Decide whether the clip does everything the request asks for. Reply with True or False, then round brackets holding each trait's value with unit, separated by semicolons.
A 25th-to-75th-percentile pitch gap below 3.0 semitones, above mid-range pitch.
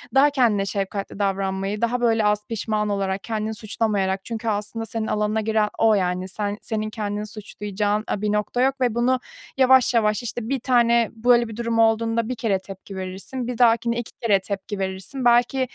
True (2.6 semitones; 220 Hz)